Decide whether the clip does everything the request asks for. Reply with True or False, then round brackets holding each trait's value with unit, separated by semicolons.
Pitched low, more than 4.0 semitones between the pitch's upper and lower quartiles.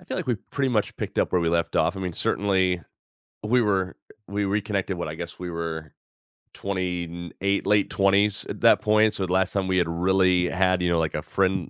False (95 Hz; 2.4 semitones)